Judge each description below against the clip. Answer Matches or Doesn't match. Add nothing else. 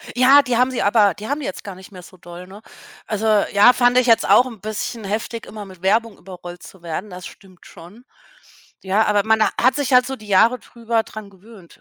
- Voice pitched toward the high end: Matches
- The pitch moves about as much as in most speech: Matches